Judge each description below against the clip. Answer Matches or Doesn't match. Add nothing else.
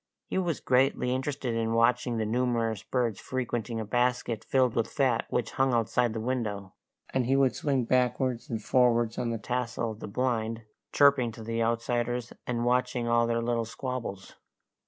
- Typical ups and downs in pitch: Doesn't match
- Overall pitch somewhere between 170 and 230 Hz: Doesn't match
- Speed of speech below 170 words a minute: Doesn't match